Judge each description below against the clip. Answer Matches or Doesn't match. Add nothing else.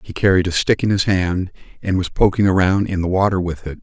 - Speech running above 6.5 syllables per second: Doesn't match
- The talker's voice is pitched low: Matches